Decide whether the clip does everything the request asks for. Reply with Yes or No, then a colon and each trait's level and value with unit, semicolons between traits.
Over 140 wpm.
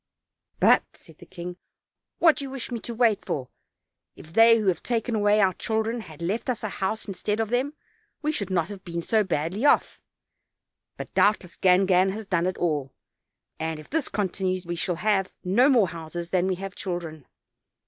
Yes: average, 190 wpm